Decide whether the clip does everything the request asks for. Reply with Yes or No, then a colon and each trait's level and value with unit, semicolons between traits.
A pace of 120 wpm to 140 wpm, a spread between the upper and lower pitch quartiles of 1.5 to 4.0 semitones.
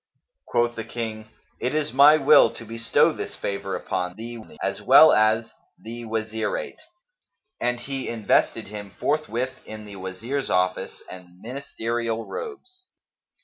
Yes: slow, 135 wpm; average, 3.3 semitones